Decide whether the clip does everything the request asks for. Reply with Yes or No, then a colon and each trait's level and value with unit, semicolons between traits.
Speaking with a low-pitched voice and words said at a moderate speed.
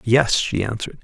Yes: low, 115 Hz; average, 175 wpm